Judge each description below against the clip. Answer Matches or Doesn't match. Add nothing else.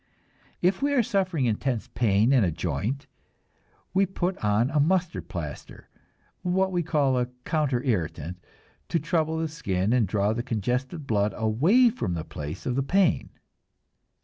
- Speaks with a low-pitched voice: Matches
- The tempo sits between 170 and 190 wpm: Doesn't match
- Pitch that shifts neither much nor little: Doesn't match